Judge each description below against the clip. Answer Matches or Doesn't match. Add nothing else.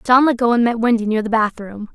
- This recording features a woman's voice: Matches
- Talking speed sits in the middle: Doesn't match